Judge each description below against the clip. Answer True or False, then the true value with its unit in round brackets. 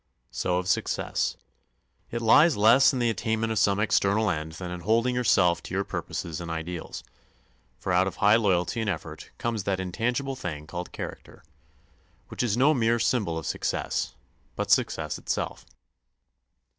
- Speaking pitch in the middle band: False (100 Hz)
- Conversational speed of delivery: True (160 wpm)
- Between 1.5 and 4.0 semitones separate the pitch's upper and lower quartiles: False (4.7 semitones)